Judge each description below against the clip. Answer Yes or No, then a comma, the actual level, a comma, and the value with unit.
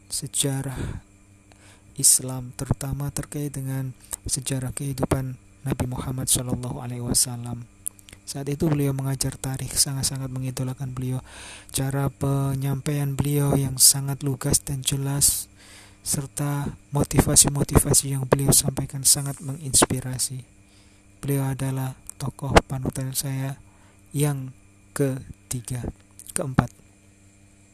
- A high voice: No, low, 130 Hz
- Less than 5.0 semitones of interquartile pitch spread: No, wide, 5.5 semitones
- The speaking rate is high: No, average, 90 wpm